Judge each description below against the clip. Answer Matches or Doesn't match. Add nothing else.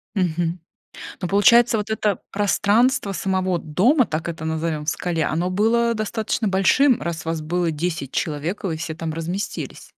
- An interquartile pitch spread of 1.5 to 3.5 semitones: Doesn't match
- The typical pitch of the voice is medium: Matches